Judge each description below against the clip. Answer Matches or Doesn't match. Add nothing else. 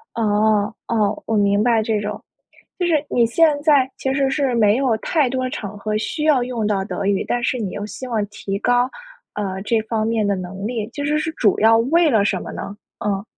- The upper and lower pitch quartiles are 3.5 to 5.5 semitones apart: Matches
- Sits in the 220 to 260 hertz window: Matches